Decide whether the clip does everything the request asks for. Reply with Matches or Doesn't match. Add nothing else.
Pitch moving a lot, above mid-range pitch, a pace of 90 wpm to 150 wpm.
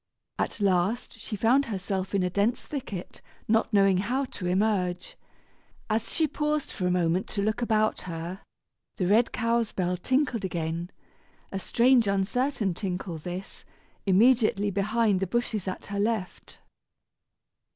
Doesn't match